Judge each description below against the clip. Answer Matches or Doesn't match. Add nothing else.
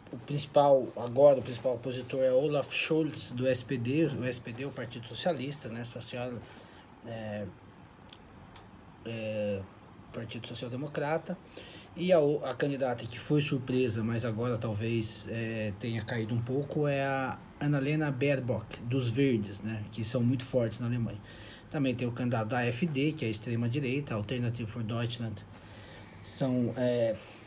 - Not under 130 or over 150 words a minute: Matches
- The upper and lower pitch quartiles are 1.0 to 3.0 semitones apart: Doesn't match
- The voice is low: Matches